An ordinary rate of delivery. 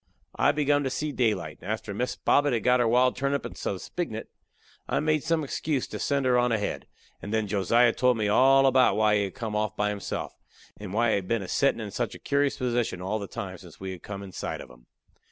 No: fast, 250 wpm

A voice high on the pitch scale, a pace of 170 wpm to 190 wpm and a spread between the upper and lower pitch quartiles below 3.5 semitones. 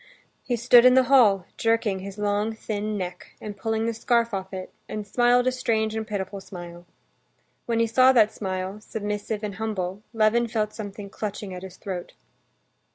Yes: high, 215 Hz; average, 175 wpm; narrow, 2.6 semitones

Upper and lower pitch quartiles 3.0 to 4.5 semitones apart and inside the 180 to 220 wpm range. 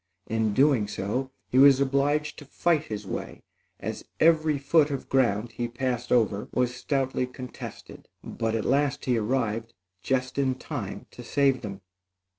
No: average, 3.4 semitones; average, 155 wpm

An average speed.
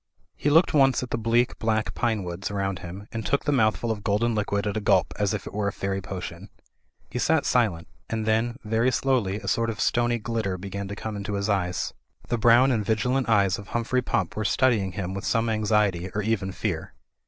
No: fast, 215 wpm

